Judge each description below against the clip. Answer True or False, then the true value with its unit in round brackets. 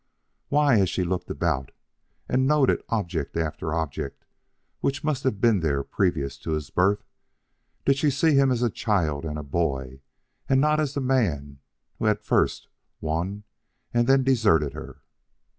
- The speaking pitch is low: True (100 Hz)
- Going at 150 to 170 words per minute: True (160 wpm)